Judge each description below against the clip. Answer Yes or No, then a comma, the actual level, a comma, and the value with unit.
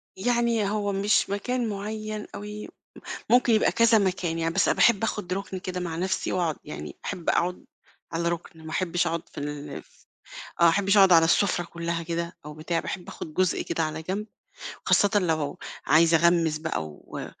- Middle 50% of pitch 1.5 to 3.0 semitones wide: No, average, 3.6 semitones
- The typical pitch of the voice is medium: Yes, medium, 180 Hz